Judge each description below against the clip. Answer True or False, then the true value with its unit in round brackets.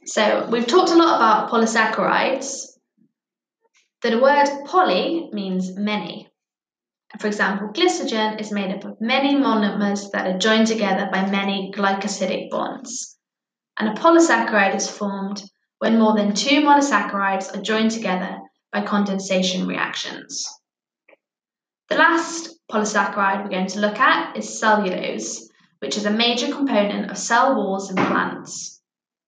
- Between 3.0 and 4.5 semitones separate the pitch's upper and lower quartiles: False (5.2 semitones)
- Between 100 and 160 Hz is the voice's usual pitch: False (210 Hz)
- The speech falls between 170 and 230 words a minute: False (135 wpm)